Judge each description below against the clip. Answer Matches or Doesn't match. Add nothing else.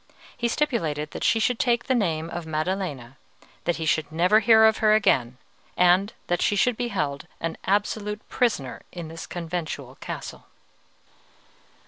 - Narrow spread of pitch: Doesn't match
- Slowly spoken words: Doesn't match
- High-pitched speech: Doesn't match